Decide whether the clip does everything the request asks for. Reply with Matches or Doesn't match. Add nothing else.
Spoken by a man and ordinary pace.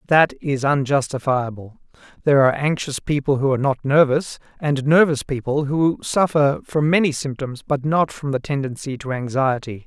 Matches